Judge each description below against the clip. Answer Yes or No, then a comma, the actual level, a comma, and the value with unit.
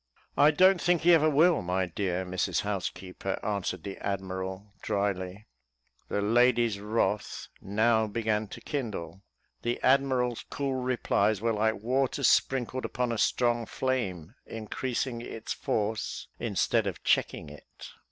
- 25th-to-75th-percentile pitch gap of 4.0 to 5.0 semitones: Yes, average, 4.3 semitones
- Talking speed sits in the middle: No, slow, 130 wpm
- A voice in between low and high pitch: No, low, 110 Hz